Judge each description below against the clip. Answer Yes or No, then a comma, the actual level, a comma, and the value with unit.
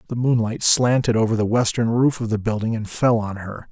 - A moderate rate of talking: No, fast, 225 wpm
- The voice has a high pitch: No, low, 115 Hz